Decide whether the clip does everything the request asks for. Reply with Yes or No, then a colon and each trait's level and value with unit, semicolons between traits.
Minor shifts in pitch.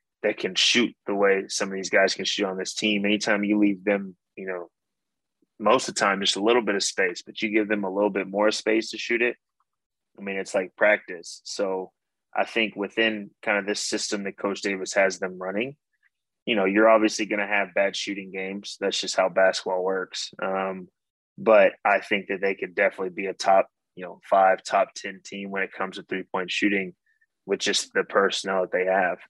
Yes: narrow, 1.9 semitones